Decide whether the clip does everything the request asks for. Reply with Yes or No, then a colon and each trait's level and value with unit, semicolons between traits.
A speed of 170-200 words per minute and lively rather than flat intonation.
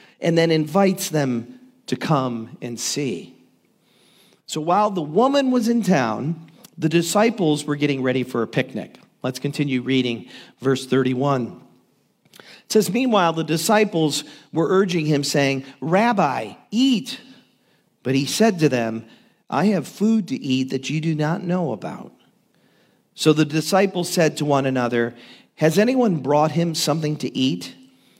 No: average, 145 wpm; wide, 7.2 semitones